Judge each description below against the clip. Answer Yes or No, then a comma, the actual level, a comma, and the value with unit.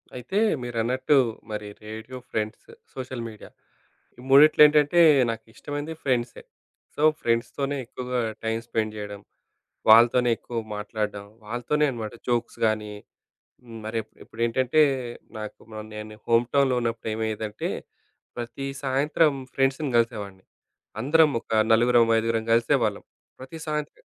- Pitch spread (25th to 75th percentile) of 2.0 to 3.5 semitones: Yes, average, 3.2 semitones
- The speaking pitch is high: No, low, 120 Hz